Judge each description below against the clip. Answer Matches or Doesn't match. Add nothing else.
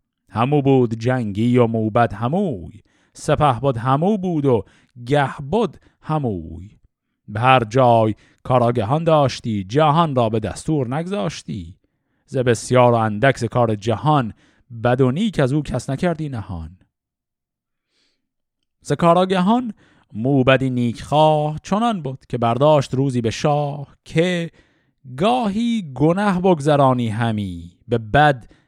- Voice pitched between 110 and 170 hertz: Matches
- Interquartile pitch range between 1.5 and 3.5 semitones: Doesn't match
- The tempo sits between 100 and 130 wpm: Matches